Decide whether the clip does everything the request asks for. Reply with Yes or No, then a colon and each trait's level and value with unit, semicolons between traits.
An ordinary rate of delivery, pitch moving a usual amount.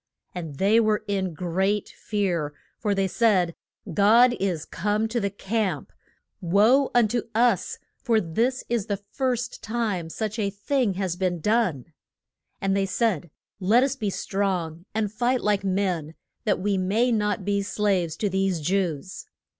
Yes: average, 155 wpm; average, 3.3 semitones